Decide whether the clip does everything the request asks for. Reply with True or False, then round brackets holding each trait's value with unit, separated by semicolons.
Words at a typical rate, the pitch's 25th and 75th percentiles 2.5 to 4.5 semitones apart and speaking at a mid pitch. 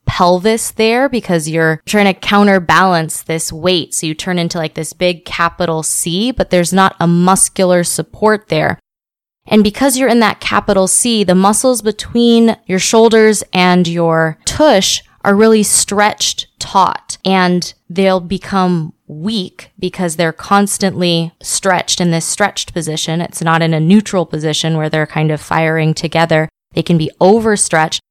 True (155 wpm; 3.8 semitones; 180 Hz)